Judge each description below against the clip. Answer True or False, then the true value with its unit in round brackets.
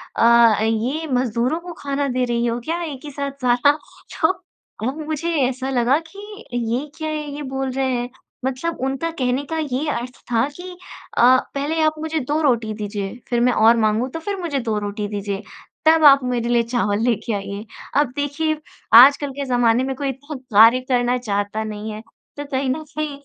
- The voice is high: True (255 Hz)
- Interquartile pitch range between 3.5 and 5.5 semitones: True (4.0 semitones)